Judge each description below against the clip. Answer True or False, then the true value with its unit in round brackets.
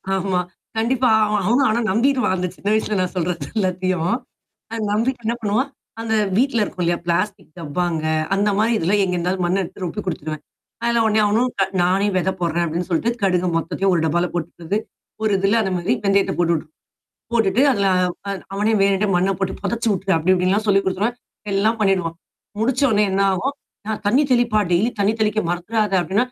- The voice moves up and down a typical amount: True (3.7 semitones)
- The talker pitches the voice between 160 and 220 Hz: True (195 Hz)